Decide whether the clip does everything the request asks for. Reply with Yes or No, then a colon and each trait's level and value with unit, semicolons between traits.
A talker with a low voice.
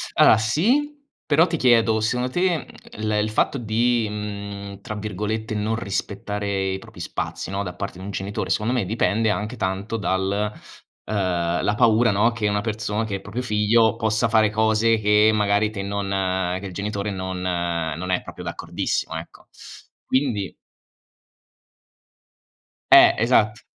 Yes: low, 105 Hz